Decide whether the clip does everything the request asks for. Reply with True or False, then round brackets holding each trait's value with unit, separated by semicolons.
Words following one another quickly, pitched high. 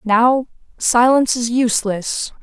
False (100 wpm; 240 Hz)